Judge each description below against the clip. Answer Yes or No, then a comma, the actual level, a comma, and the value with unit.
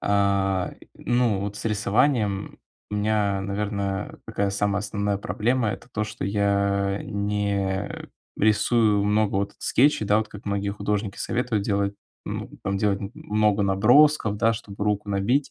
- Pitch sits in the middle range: No, low, 105 Hz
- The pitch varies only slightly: Yes, narrow, 1.4 semitones